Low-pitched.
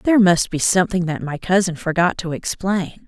No: medium, 180 Hz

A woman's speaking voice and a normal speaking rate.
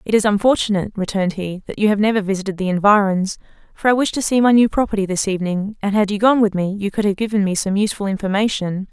No: female; fast, 240 wpm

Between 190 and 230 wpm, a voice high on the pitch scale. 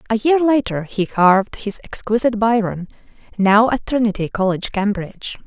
No: average, 145 wpm; high, 215 Hz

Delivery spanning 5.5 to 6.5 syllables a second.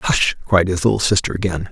Yes: 5.7 syllables/s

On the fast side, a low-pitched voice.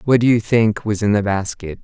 Yes: fast, 260 wpm; low, 110 Hz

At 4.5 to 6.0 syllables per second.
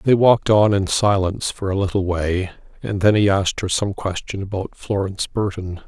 Yes: 5.3 syllables/s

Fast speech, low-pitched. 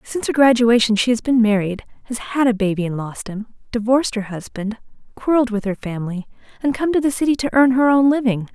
No: fast, 220 wpm; high, 235 Hz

